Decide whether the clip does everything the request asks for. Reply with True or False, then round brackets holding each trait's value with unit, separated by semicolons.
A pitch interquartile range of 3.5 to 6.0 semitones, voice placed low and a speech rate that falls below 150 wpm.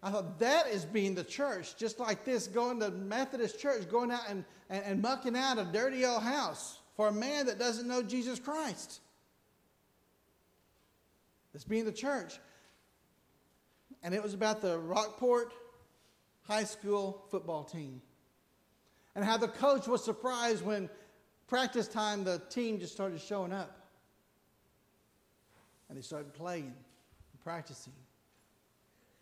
False (4.1 semitones; 215 Hz; 140 wpm)